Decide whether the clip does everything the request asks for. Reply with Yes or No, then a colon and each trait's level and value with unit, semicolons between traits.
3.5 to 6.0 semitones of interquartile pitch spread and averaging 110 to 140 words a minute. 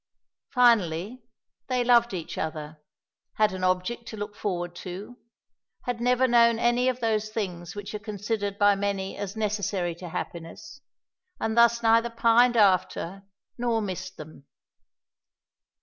Yes: average, 4.2 semitones; slow, 135 wpm